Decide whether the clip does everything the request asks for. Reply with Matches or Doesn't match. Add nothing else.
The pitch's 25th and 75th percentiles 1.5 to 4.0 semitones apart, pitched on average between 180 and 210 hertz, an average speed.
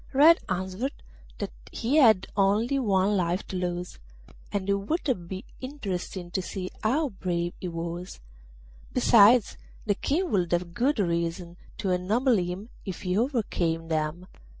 Doesn't match